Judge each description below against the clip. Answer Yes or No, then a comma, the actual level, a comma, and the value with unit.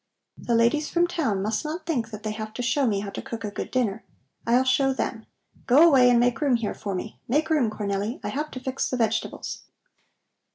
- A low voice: No, high, 240 Hz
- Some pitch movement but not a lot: Yes, average, 3.9 semitones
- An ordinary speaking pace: No, fast, 220 wpm